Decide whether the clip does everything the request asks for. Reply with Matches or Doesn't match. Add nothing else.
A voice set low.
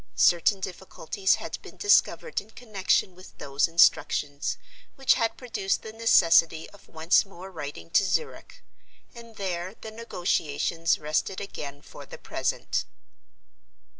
Doesn't match